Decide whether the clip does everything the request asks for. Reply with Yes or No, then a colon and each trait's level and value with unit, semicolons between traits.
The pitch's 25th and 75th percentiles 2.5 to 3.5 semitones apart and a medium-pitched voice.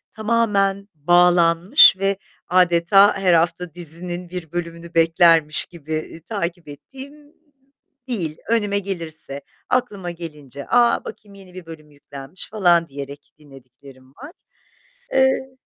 No: average, 3.9 semitones; medium, 175 Hz